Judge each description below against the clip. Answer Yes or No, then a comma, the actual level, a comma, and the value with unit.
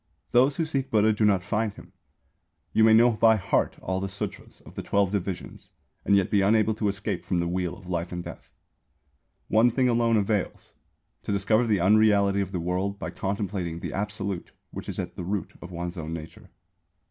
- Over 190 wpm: Yes, average, 200 wpm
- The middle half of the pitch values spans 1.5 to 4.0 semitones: Yes, average, 3.0 semitones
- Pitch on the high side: No, low, 100 Hz